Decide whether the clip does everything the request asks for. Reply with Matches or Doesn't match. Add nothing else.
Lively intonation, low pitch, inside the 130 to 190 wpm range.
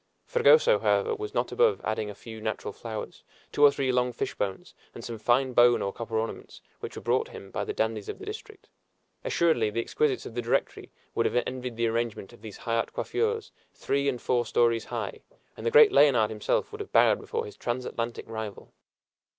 Doesn't match